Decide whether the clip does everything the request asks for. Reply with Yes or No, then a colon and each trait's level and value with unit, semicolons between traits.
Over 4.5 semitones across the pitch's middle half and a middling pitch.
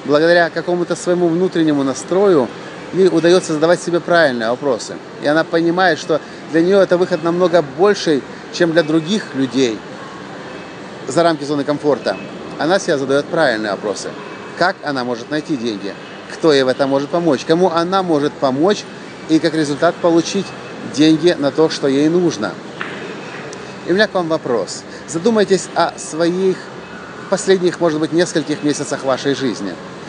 No: average, 3.1 semitones; medium, 165 Hz